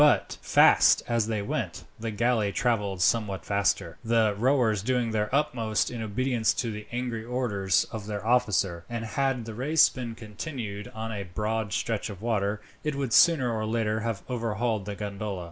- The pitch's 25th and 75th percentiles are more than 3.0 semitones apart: No, average, 2.7 semitones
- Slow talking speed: No, average, 175 wpm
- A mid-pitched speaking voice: No, low, 110 Hz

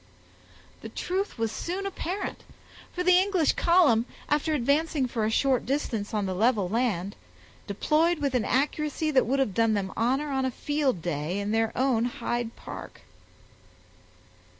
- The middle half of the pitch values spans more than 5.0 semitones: Yes, wide, 5.5 semitones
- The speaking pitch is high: Yes, very high, 255 Hz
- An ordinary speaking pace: Yes, average, 155 wpm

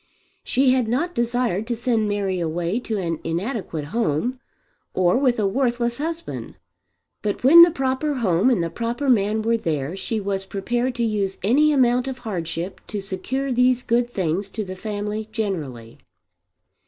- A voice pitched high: Yes, high, 220 Hz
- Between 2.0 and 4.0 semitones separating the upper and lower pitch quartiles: No, average, 4.7 semitones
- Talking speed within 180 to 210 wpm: No, average, 165 wpm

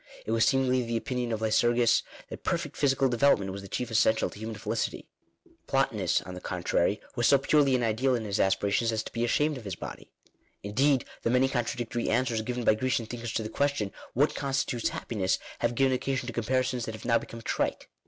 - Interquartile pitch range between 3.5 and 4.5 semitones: No, average, 2.8 semitones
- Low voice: Yes, low, 120 Hz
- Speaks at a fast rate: Yes, fast, 215 wpm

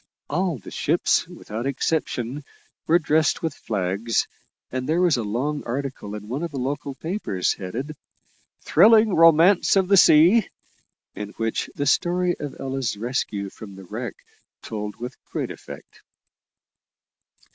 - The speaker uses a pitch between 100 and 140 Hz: Yes, low, 135 Hz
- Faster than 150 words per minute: No, average, 140 wpm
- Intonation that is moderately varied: No, wide, 6.5 semitones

